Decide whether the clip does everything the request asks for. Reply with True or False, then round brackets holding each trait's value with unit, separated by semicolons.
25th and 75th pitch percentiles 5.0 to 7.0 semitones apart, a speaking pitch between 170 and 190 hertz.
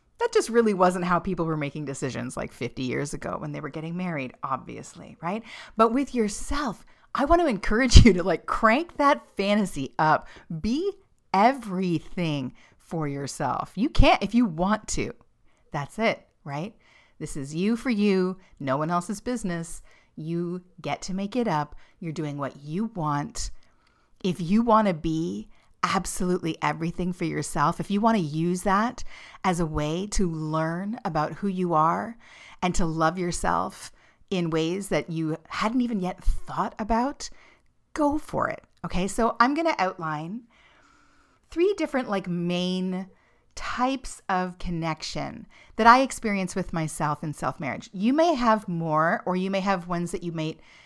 True (5.6 semitones; 185 Hz)